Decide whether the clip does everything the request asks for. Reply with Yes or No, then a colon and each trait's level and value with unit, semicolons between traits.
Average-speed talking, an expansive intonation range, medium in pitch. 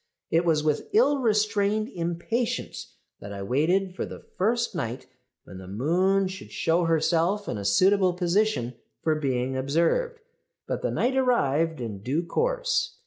Yes: average, 150 wpm; wide, 7.0 semitones; medium, 175 Hz